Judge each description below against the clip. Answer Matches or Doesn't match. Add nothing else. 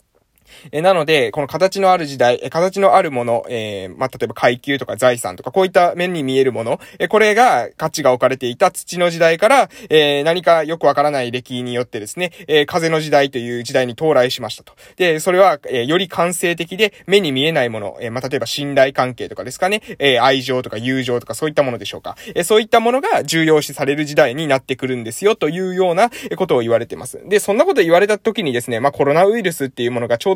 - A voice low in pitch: Doesn't match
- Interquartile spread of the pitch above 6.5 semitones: Doesn't match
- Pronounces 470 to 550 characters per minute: Matches